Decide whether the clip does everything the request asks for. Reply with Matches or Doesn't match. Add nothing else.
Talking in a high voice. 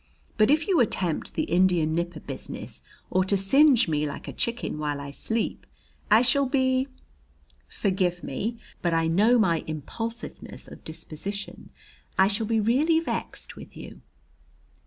Matches